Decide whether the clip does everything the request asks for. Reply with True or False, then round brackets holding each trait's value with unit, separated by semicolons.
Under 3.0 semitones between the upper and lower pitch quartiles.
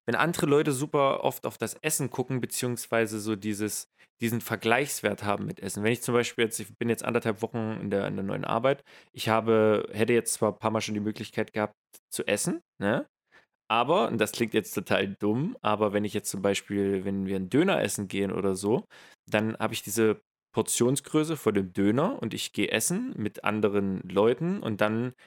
True (2.6 semitones)